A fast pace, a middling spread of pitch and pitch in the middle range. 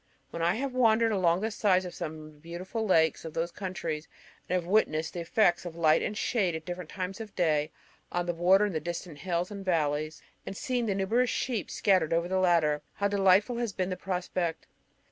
Yes: fast, 215 wpm; average, 3.5 semitones; medium, 180 Hz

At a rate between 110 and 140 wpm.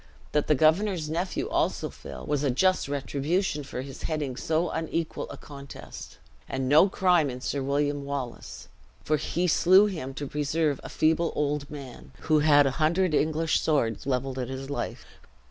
No: average, 170 wpm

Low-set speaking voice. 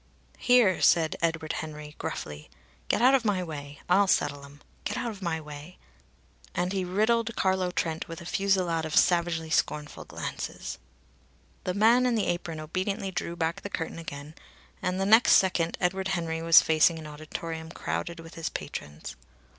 No: medium, 170 Hz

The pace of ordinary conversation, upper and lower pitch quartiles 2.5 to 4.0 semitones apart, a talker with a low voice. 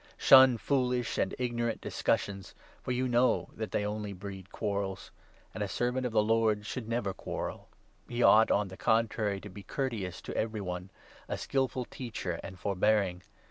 Yes: average, 180 wpm; average, 3.6 semitones; low, 110 Hz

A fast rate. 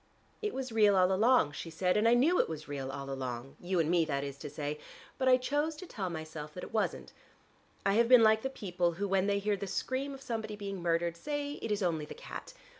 Yes: fast, 250 wpm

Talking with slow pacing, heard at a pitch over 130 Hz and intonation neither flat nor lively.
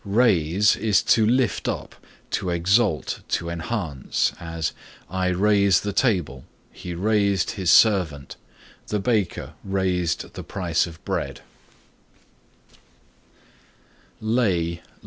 No: slow, 100 wpm; very low, 95 Hz; average, 3.6 semitones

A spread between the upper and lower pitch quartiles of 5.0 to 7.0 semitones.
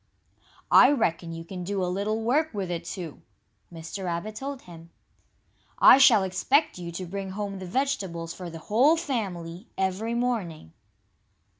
Yes: wide, 5.5 semitones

